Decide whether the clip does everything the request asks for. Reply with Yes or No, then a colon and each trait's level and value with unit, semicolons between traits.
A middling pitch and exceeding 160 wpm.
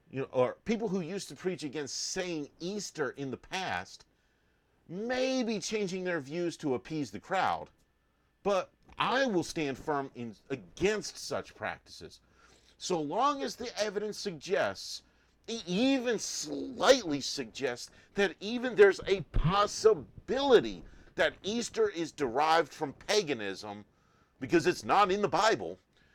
No: medium, 180 Hz; slow, 135 wpm